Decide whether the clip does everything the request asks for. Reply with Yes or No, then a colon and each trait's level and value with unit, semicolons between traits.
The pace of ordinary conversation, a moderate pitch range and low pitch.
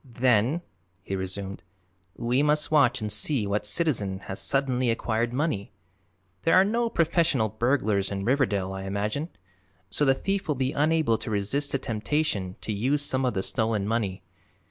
No: average, 165 wpm; wide, 6.0 semitones; low, 120 Hz